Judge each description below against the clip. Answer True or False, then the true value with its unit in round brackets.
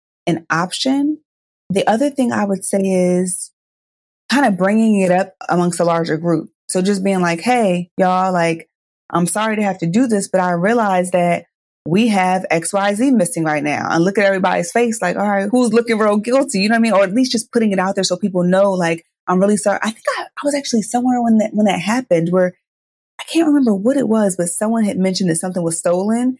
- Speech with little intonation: False (4.3 semitones)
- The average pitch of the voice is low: False (195 Hz)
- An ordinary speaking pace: False (230 wpm)